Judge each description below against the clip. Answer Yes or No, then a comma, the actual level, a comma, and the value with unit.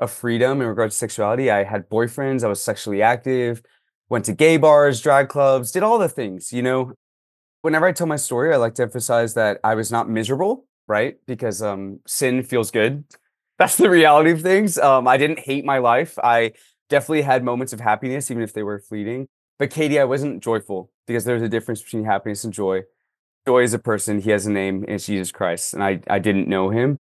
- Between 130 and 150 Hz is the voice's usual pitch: No, low, 120 Hz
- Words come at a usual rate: No, fast, 215 wpm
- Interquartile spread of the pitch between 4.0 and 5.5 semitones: Yes, average, 4.3 semitones